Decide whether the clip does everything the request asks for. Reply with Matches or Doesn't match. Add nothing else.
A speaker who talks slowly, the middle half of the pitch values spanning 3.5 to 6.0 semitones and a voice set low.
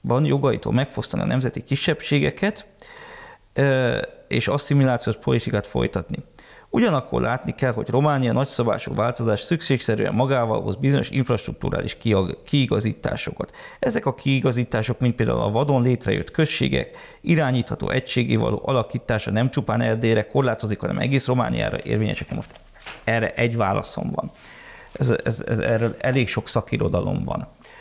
Doesn't match